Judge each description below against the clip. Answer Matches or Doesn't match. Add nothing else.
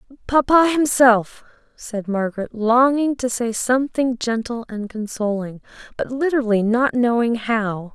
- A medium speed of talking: Doesn't match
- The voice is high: Matches